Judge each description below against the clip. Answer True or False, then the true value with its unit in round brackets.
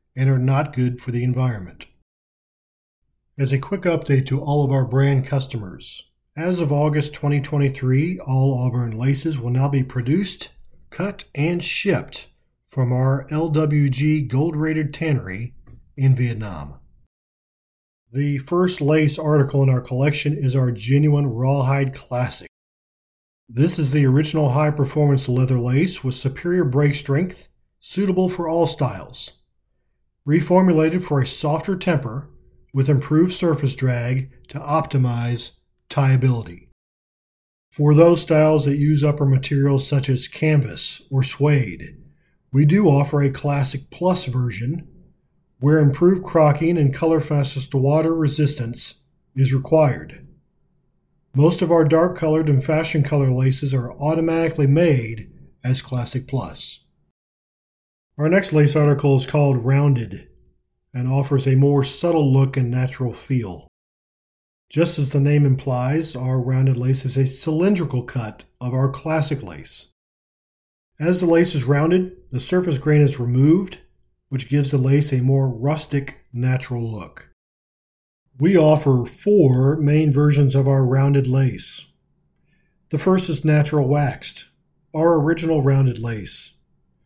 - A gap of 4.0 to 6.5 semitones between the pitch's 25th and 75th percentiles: False (3.2 semitones)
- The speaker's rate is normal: False (130 wpm)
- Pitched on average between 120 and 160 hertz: True (140 Hz)